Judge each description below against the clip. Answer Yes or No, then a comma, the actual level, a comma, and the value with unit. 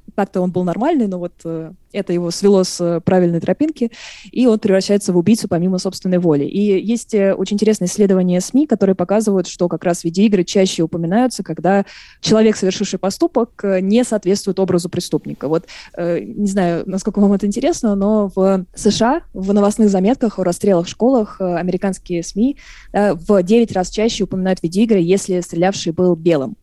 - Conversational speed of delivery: No, fast, 165 wpm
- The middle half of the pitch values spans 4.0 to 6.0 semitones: No, average, 2.9 semitones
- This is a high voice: Yes, high, 195 Hz